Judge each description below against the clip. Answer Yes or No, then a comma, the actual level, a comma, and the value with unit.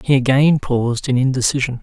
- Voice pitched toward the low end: Yes, low, 130 Hz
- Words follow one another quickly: No, average, 165 wpm